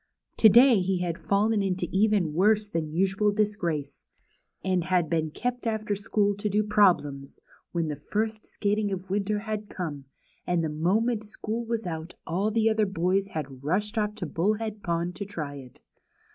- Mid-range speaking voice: No, high, 200 Hz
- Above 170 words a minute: Yes, average, 180 wpm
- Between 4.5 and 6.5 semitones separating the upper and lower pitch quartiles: No, average, 4.0 semitones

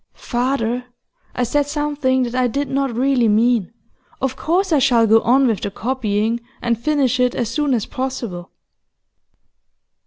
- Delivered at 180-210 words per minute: No, average, 155 wpm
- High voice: Yes, very high, 250 Hz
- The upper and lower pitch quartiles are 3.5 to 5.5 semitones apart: No, average, 3.0 semitones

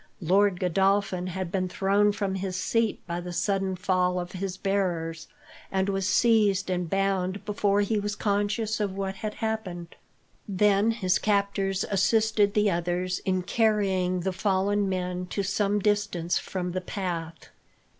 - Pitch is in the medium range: No, high, 195 Hz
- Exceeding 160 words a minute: No, average, 150 wpm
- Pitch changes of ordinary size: No, narrow, 2.0 semitones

